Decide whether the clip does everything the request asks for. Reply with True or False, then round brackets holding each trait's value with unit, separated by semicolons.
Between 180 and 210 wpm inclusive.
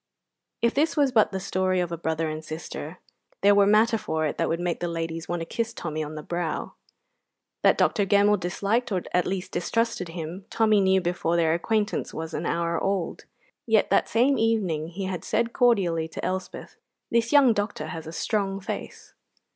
True (195 wpm)